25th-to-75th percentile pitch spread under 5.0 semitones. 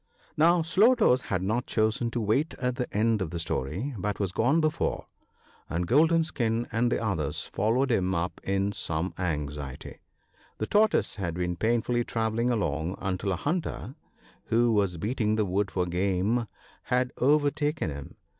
No: wide, 5.4 semitones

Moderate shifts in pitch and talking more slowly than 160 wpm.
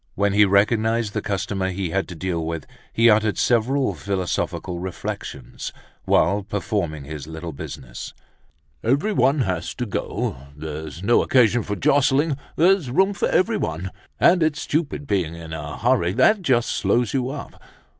No: wide, 7.0 semitones; average, 150 wpm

